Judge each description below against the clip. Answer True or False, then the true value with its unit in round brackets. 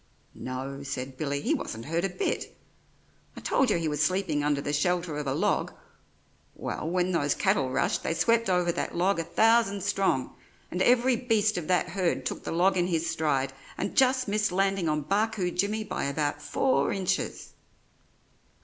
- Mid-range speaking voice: True (175 Hz)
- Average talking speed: True (180 wpm)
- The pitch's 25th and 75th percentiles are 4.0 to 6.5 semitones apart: True (5.2 semitones)